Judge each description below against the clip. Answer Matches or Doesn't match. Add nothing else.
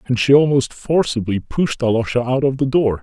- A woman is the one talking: Doesn't match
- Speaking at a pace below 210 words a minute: Matches